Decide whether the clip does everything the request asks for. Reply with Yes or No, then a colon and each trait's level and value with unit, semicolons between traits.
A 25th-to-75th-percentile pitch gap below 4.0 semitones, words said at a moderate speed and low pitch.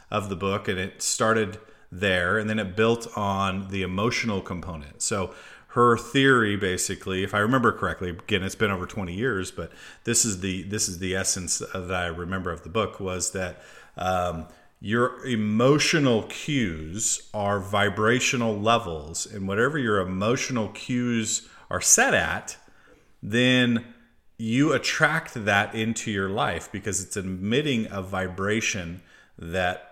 Yes: average, 3.5 semitones; average, 150 wpm; low, 100 Hz